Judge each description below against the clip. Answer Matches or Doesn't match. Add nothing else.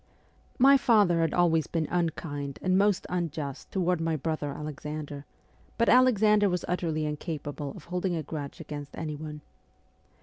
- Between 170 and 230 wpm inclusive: Doesn't match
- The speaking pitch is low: Doesn't match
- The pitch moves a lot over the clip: Doesn't match